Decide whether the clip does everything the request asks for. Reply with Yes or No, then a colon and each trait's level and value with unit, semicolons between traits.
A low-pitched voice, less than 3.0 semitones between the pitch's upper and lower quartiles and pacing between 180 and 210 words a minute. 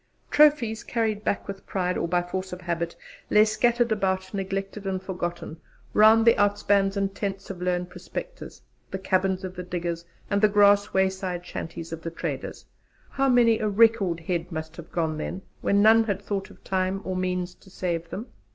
No: high, 190 Hz; narrow, 2.6 semitones; average, 185 wpm